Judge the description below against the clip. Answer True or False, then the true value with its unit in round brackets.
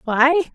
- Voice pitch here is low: False (285 Hz)